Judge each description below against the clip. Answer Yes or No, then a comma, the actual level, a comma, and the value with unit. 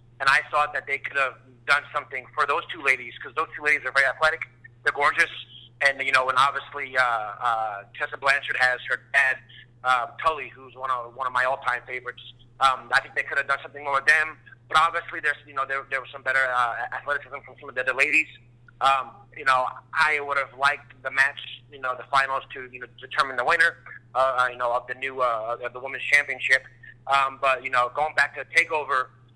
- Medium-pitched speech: No, low, 130 Hz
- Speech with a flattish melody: Yes, narrow, 2.3 semitones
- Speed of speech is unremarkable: No, fast, 225 wpm